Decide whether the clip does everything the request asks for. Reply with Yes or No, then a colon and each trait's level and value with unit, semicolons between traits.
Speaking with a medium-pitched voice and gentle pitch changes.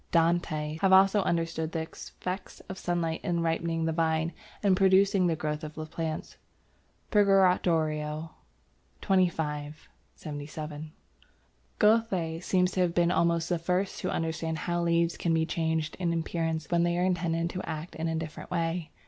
Yes: medium, 165 Hz; narrow, 2.0 semitones